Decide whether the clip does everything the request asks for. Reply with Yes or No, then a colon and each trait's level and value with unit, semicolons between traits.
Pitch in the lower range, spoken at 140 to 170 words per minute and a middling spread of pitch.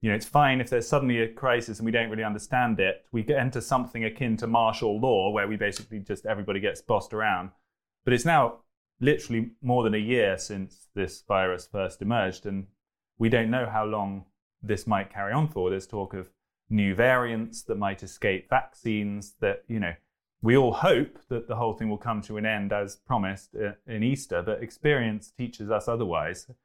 No: low, 110 Hz; average, 200 wpm; average, 3.2 semitones